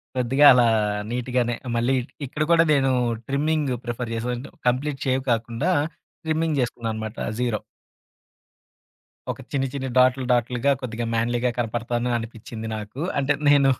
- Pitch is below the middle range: Yes, low, 125 Hz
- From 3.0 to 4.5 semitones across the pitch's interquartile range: No, narrow, 2.6 semitones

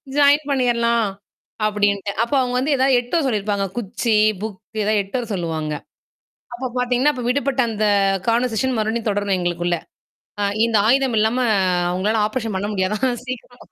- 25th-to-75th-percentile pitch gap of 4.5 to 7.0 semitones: No, average, 3.7 semitones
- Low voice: No, high, 230 Hz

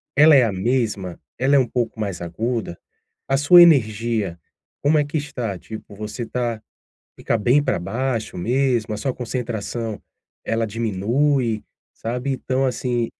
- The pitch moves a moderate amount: Yes, average, 3.5 semitones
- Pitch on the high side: No, low, 120 Hz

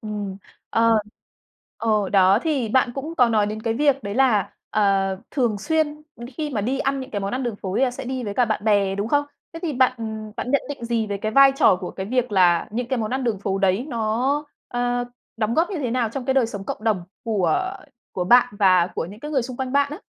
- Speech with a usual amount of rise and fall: Yes, average, 4.4 semitones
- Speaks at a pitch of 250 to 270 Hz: No, high, 235 Hz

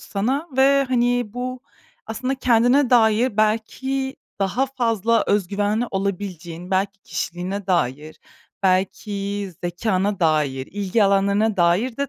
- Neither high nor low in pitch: No, high, 205 Hz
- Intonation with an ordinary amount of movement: Yes, average, 4.5 semitones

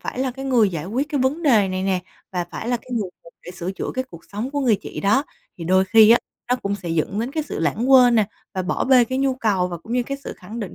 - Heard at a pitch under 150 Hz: No, high, 225 Hz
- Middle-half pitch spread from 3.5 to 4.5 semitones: No, wide, 5.5 semitones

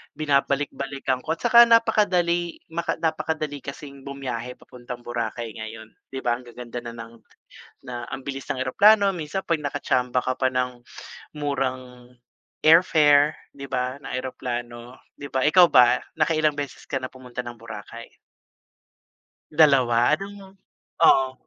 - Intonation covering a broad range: No, average, 3.7 semitones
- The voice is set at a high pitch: No, low, 135 Hz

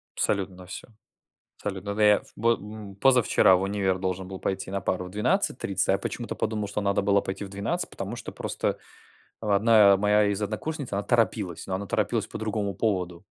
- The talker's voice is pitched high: No, low, 100 Hz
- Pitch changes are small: Yes, narrow, 1.8 semitones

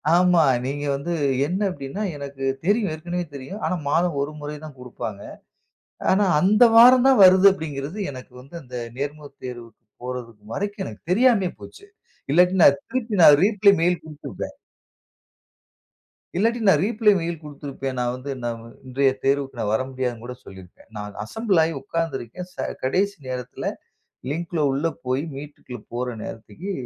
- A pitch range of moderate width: No, wide, 6.3 semitones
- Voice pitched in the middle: Yes, medium, 150 Hz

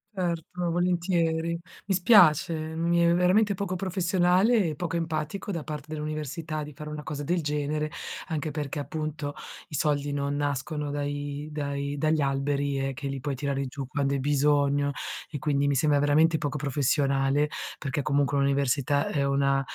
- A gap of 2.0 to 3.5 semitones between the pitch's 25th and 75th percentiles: Yes, narrow, 2.6 semitones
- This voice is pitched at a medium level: Yes, medium, 150 Hz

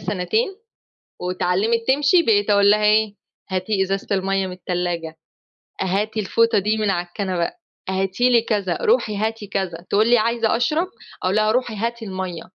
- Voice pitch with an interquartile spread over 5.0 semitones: No, average, 3.3 semitones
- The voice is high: Yes, high, 205 Hz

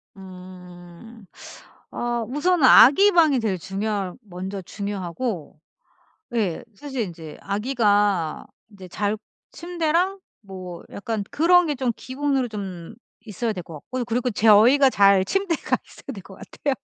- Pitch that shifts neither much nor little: No, wide, 6.0 semitones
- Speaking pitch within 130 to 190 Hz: No, high, 210 Hz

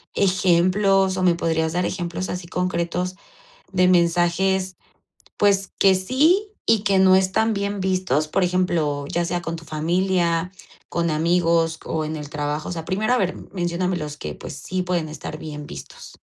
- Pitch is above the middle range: No, medium, 180 Hz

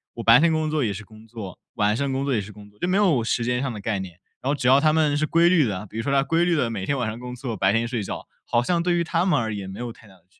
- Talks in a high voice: No, low, 120 Hz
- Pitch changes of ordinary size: No, wide, 6.0 semitones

